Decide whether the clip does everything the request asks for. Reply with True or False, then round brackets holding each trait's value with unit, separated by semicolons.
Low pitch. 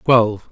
True (115 Hz)